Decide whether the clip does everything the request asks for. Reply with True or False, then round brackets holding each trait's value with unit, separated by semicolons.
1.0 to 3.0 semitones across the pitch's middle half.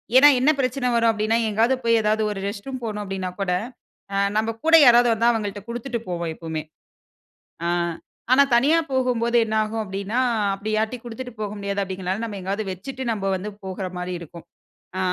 False (3.5 semitones)